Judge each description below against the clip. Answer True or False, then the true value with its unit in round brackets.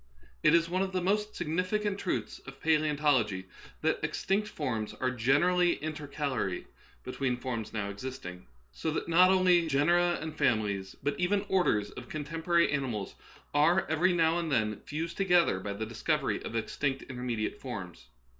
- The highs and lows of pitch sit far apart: True (6.8 semitones)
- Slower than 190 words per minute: True (160 wpm)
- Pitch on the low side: False (150 Hz)